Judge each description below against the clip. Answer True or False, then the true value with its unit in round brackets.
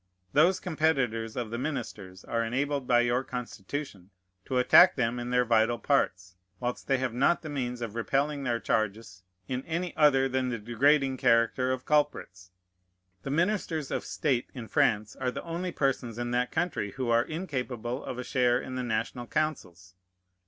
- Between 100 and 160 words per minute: False (175 wpm)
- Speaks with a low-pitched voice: True (125 Hz)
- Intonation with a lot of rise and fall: False (3.5 semitones)